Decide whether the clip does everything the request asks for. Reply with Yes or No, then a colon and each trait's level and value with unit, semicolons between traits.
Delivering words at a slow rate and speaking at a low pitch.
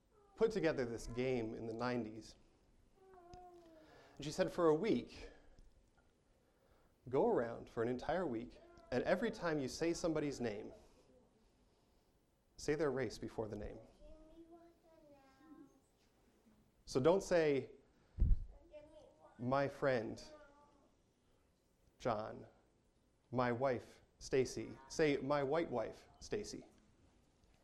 No: slow, 100 wpm; medium, 165 Hz